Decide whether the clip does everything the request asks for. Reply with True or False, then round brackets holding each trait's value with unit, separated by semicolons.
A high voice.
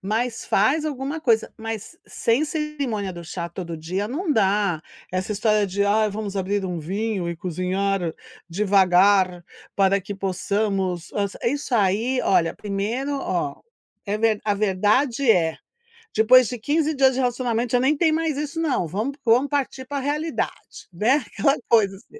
True (215 Hz)